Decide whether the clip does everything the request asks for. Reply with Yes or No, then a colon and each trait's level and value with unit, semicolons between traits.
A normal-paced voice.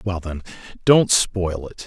Yes: average, 160 wpm